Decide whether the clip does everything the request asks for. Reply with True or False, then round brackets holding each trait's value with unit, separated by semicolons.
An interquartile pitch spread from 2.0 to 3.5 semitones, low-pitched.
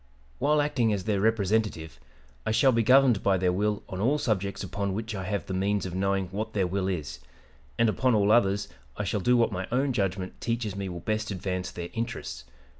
True (3.2 semitones; 100 Hz)